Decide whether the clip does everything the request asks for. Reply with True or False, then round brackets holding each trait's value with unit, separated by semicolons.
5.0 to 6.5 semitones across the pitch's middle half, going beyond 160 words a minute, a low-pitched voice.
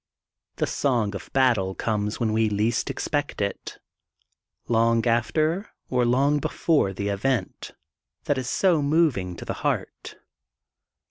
False (5.3 semitones; 140 wpm; 120 Hz)